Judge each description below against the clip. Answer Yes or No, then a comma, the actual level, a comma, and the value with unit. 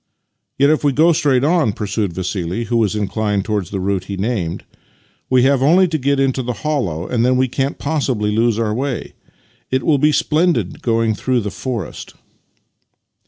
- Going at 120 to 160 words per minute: No, average, 190 wpm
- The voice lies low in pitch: Yes, low, 120 Hz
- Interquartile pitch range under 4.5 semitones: No, average, 5.2 semitones